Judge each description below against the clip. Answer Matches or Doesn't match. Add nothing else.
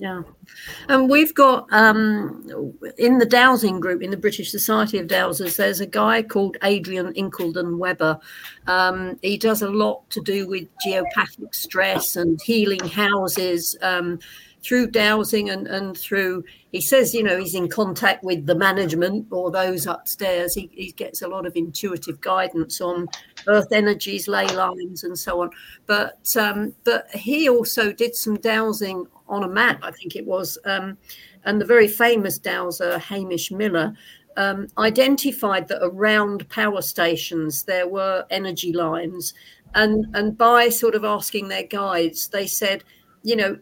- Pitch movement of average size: Matches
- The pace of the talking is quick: Doesn't match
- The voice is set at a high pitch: Matches